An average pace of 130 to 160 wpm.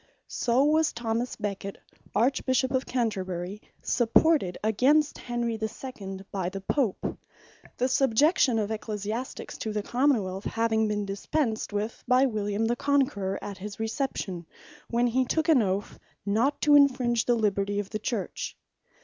Yes: average, 150 wpm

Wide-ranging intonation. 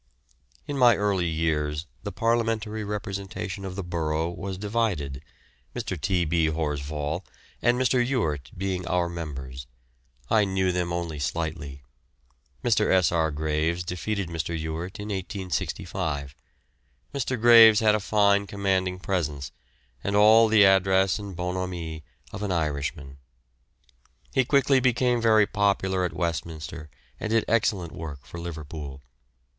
No: average, 4.6 semitones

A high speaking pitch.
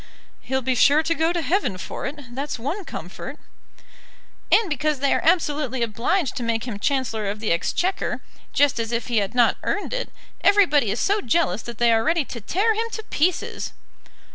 Yes: very high, 275 Hz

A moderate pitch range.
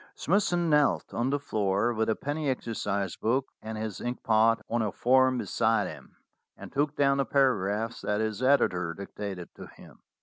Yes: average, 4.5 semitones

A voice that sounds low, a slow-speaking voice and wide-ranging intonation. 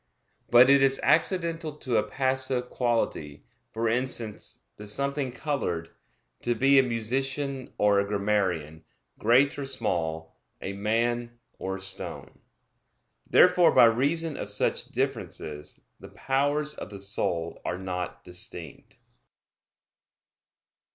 Yes: low, 120 Hz; slow, 120 wpm; wide, 5.8 semitones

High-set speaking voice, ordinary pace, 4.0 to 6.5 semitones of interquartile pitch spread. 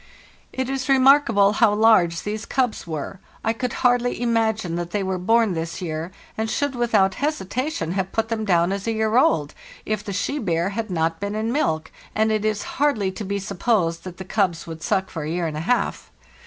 No: high, 205 Hz; fast, 210 wpm; average, 4.5 semitones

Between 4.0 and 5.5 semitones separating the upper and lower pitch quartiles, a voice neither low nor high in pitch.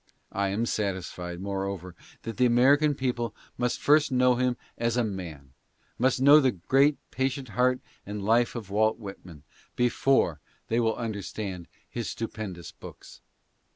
No: average, 4.5 semitones; low, 115 Hz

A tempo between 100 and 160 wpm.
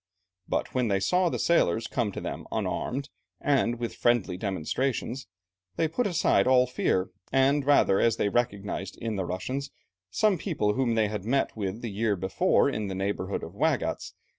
No: average, 175 wpm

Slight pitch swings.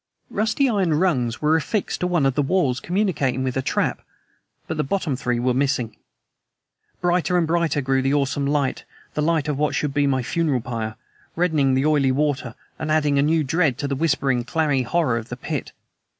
No: average, 3.8 semitones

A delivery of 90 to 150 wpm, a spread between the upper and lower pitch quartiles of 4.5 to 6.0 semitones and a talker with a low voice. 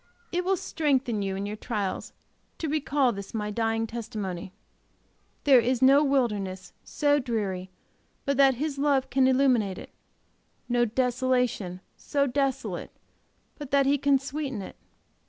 No: average, 140 wpm; average, 4.8 semitones; very high, 255 Hz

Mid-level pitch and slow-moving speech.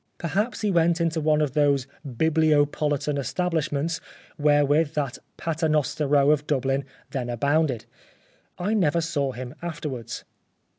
Yes: medium, 150 Hz; slow, 120 wpm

